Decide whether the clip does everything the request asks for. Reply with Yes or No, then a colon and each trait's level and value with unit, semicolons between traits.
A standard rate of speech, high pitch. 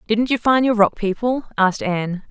No: fast, 210 wpm; high, 220 Hz